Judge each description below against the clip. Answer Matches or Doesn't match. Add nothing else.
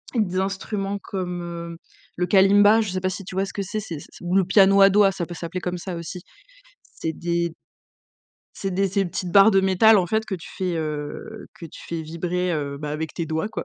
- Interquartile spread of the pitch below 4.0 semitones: Matches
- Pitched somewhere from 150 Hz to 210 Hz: Matches